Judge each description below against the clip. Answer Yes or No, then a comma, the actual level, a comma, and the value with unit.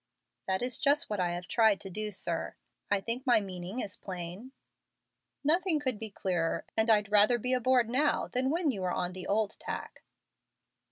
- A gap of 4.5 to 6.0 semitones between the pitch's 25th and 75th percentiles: Yes, average, 5.1 semitones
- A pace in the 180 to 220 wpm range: Yes, average, 185 wpm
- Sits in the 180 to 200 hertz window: No, high, 215 Hz